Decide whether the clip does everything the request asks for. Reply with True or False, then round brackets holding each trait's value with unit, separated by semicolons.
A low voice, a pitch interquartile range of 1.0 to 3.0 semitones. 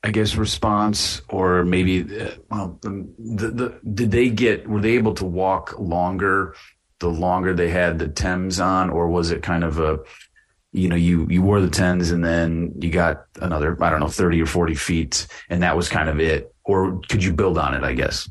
True (90 Hz; 2.7 semitones)